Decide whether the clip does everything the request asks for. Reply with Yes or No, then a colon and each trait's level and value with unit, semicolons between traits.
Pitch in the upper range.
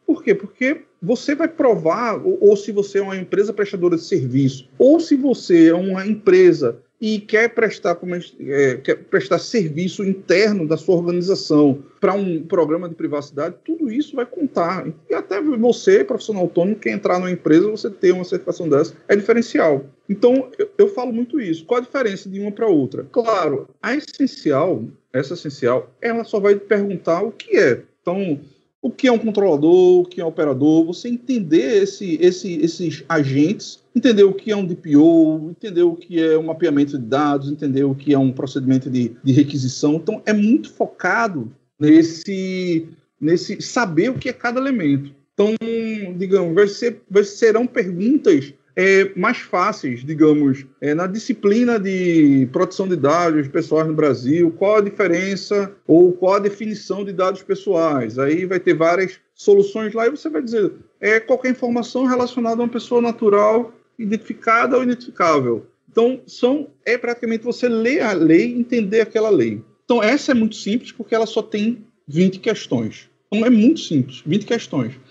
Yes: high, 200 Hz